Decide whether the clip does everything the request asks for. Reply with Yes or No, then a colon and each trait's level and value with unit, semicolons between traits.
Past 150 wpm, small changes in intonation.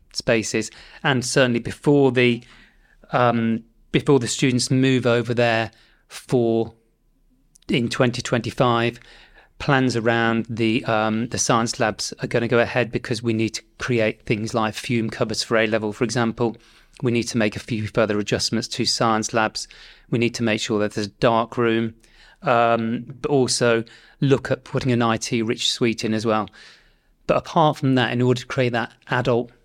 Yes: average, 175 wpm; narrow, 1.7 semitones